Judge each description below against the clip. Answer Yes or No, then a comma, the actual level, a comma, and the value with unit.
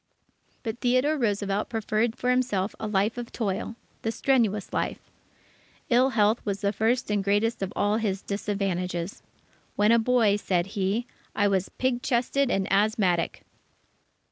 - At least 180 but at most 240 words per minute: No, average, 145 wpm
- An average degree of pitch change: Yes, average, 3.1 semitones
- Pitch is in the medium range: No, high, 210 Hz